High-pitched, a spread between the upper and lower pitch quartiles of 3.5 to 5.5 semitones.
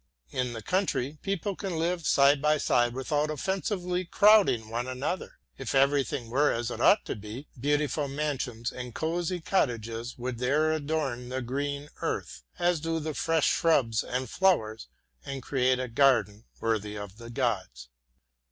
No: low, 135 Hz; average, 4.9 semitones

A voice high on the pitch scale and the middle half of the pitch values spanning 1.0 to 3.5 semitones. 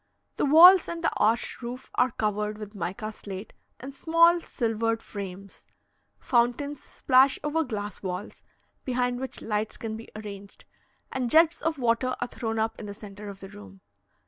No: high, 230 Hz; average, 4.1 semitones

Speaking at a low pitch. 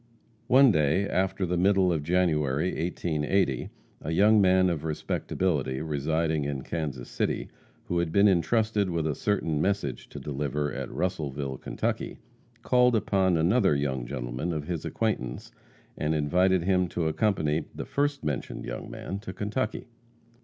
Yes: very low, 85 Hz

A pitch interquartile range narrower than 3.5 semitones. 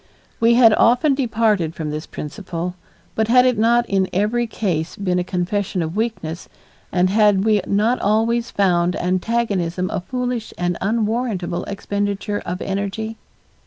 No: average, 4.1 semitones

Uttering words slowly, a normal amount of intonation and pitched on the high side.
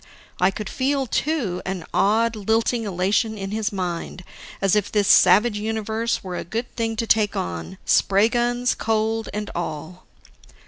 No: average, 155 wpm; average, 3.0 semitones; high, 215 Hz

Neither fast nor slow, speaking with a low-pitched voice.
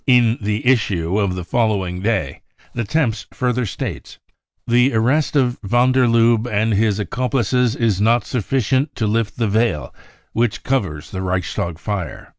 Yes: average, 160 wpm; low, 115 Hz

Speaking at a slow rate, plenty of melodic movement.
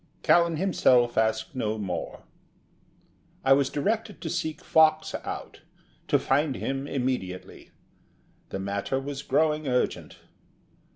Yes: slow, 115 wpm; wide, 5.7 semitones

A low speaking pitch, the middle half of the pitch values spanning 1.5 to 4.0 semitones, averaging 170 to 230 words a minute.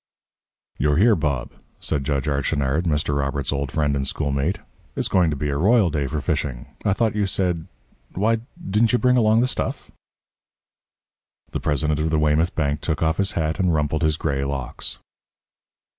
No: very low, 75 Hz; average, 4.4 semitones; average, 175 wpm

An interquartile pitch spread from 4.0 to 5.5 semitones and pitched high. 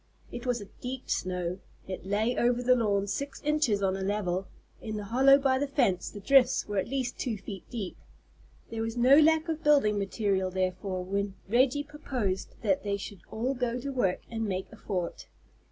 Yes: average, 5.1 semitones; high, 220 Hz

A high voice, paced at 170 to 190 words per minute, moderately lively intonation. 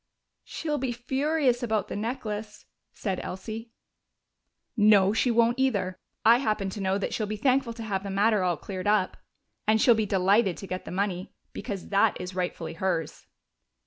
Yes: high, 210 Hz; average, 175 wpm; average, 3.6 semitones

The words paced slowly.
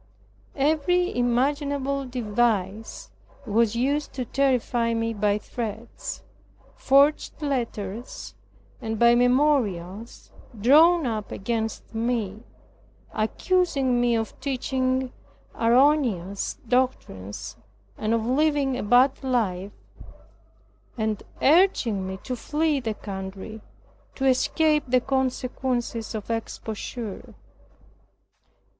Yes: slow, 90 wpm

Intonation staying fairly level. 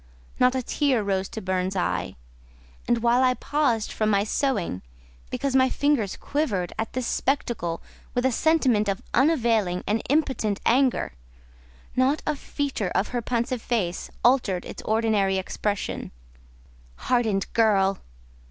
No: average, 4.7 semitones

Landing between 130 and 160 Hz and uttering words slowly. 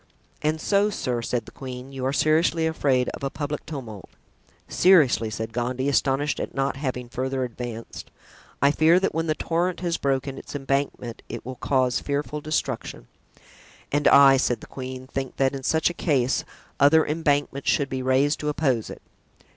No: low, 135 Hz; average, 175 wpm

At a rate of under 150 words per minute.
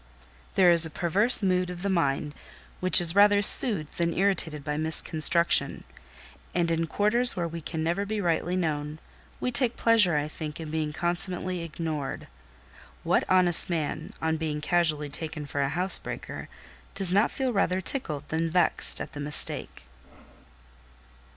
No: average, 155 wpm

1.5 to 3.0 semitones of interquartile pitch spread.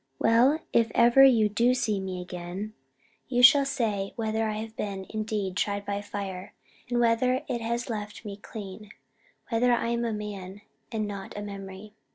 Yes: average, 2.7 semitones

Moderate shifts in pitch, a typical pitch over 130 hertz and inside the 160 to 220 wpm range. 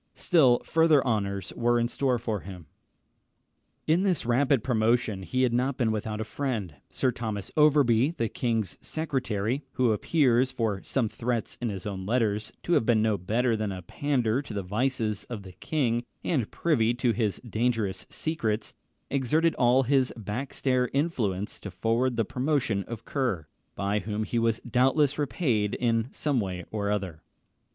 No: average, 3.8 semitones; low, 115 Hz; average, 165 wpm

